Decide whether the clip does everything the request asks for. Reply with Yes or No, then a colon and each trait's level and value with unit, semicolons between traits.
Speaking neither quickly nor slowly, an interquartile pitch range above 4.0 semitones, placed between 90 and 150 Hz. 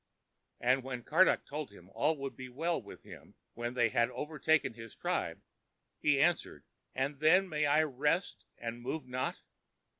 Yes: average, 160 wpm; average, 4.4 semitones; medium, 140 Hz